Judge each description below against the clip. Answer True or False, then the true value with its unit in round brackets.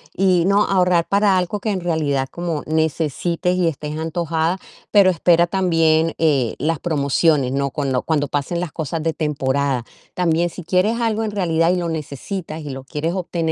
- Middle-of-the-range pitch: True (165 Hz)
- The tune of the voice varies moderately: True (3.3 semitones)